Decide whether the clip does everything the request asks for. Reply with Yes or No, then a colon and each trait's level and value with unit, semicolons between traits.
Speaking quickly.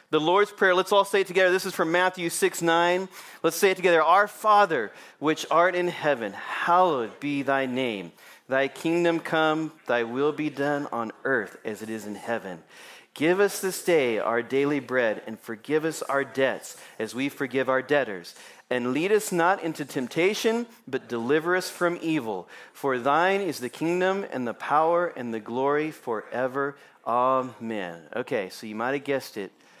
No: average, 180 wpm